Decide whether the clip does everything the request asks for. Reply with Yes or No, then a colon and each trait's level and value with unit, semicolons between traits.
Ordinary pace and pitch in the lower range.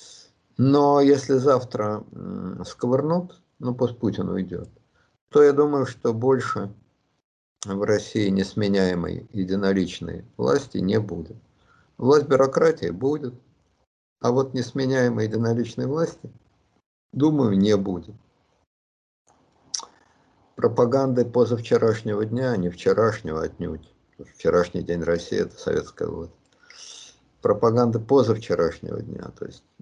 No: slow, 100 wpm; low, 115 Hz